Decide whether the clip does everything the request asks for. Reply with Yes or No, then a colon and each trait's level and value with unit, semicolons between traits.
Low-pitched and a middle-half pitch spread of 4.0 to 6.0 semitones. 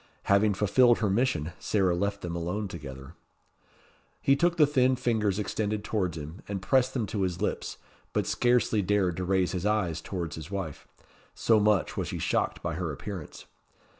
No: low, 100 Hz; average, 3.6 semitones